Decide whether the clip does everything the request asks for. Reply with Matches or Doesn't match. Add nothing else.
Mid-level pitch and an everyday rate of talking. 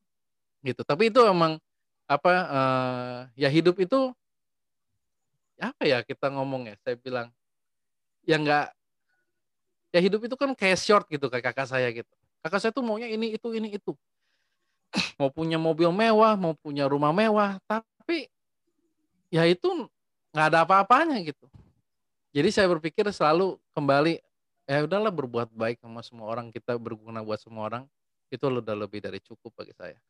Doesn't match